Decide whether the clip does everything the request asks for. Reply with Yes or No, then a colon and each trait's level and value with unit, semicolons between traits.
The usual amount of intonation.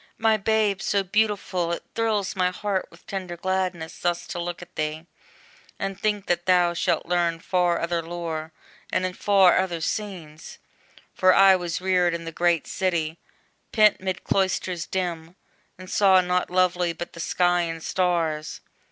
No: narrow, 1.8 semitones